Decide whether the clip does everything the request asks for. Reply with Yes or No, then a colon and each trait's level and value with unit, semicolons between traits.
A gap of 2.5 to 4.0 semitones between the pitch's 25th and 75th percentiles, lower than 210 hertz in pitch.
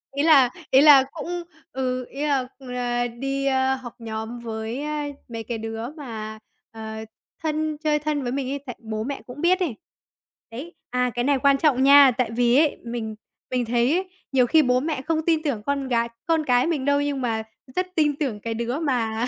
No: average, 3.6 semitones; very high, 260 Hz